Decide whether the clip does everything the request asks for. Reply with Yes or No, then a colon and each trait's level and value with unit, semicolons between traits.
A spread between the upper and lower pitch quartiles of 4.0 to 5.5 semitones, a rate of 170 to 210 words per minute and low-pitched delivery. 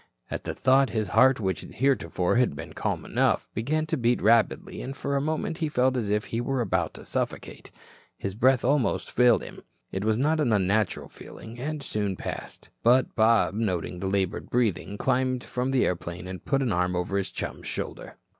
Yes: average, 5.1 semitones; average, 195 wpm; low, 115 Hz